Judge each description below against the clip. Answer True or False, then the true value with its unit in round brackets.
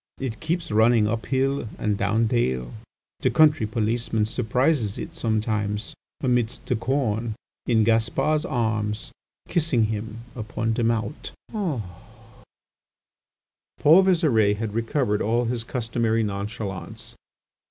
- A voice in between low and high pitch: False (115 Hz)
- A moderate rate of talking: False (110 wpm)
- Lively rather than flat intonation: False (2.7 semitones)